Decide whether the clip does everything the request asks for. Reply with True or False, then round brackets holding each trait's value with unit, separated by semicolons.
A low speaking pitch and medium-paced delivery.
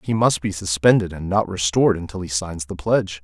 False (90 Hz; 225 wpm)